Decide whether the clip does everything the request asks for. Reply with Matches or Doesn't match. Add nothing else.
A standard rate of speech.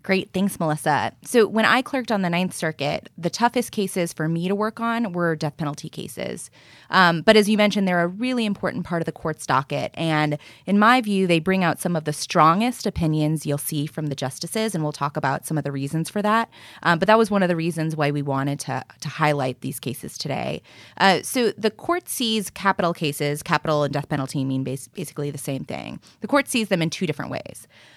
Doesn't match